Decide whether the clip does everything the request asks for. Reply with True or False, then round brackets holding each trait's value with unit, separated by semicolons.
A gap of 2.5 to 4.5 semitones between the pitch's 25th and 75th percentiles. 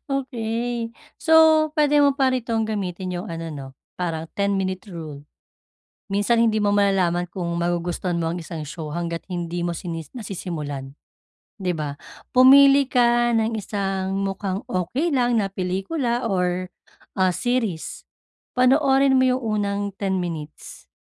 False (5.6 semitones)